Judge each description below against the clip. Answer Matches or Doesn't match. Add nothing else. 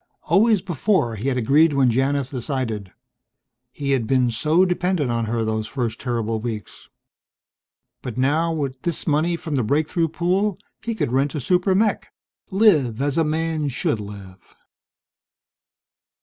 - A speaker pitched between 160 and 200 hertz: Doesn't match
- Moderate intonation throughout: Doesn't match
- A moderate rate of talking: Matches